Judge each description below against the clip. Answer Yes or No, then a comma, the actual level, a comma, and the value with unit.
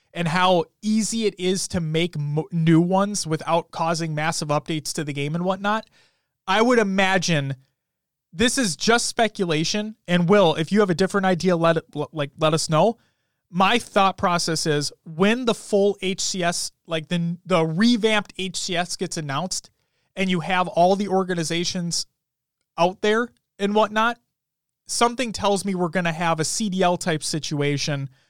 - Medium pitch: Yes, medium, 175 Hz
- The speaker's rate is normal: Yes, average, 160 wpm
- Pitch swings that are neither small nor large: Yes, average, 3.9 semitones